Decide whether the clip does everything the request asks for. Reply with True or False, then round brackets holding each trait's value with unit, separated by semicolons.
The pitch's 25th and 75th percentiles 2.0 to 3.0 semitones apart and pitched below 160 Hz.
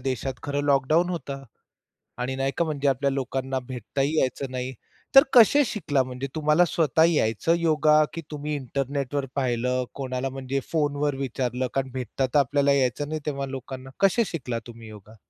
True (2.7 semitones; 135 Hz)